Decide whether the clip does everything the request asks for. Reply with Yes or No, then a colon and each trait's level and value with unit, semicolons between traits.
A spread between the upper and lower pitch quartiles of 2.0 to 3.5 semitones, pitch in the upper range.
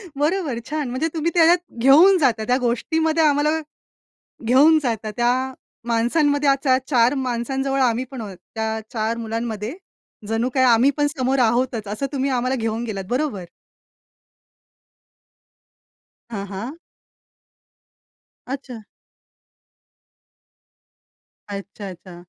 No: average, 4.1 semitones; very high, 250 Hz